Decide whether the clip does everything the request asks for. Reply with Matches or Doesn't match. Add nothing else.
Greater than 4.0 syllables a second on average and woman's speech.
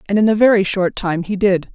Matches